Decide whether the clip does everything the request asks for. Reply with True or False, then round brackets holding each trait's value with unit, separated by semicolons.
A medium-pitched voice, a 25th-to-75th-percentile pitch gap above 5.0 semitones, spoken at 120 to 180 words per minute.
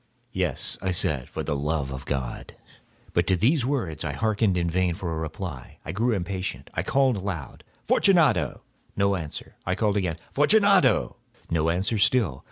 False (95 Hz; 5.6 semitones; 170 wpm)